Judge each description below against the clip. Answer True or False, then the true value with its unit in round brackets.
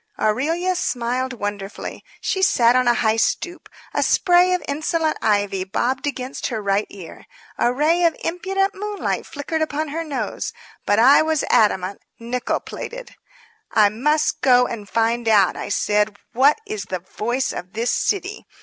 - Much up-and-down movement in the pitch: True (7.1 semitones)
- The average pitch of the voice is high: True (255 Hz)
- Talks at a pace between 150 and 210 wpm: True (160 wpm)